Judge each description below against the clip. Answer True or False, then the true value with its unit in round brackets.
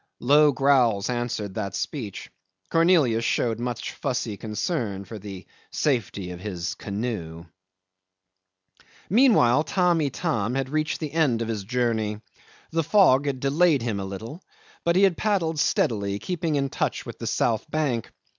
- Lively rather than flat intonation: True (6.6 semitones)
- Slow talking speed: False (145 wpm)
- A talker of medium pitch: False (125 Hz)